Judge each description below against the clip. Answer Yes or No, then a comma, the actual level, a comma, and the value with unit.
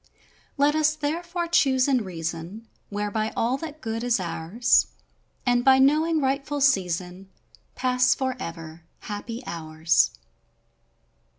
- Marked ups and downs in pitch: Yes, wide, 7.3 semitones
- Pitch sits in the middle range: No, high, 245 Hz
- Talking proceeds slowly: Yes, slow, 115 wpm